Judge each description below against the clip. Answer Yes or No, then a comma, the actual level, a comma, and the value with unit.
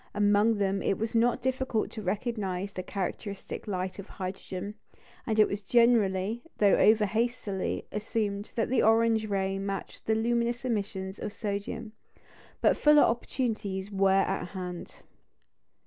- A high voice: Yes, high, 205 Hz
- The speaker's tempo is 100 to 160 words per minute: Yes, average, 140 wpm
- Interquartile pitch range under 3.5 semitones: Yes, average, 2.8 semitones